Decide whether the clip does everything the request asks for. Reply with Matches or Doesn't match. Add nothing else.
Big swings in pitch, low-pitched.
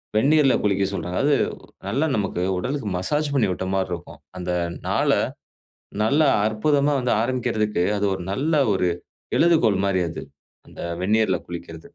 Matches